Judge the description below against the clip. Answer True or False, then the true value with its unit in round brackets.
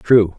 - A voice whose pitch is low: True (100 Hz)